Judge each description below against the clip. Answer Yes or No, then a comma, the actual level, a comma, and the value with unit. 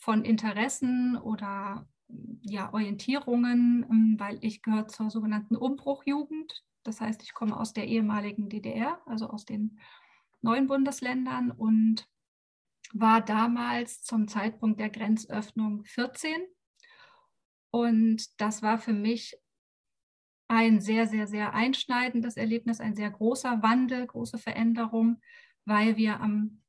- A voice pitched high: Yes, high, 225 Hz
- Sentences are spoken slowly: Yes, slow, 115 wpm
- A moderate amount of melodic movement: No, narrow, 2.2 semitones